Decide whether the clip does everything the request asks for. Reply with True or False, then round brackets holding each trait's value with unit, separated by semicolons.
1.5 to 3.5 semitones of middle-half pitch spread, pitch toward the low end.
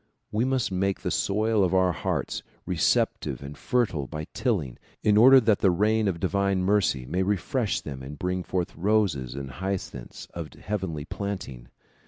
False (5.3 semitones; 95 Hz)